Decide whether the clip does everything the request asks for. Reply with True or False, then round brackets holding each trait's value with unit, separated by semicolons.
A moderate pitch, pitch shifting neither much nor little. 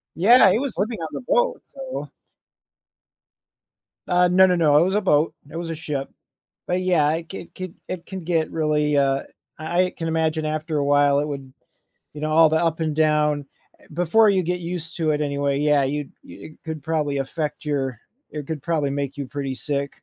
True (155 Hz; 3.2 semitones)